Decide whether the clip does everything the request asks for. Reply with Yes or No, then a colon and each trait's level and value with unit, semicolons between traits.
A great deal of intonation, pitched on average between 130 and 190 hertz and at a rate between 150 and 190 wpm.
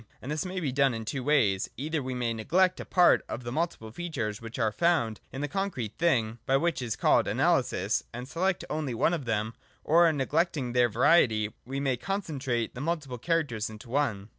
No: wide, 5.9 semitones; low, 135 Hz; average, 200 wpm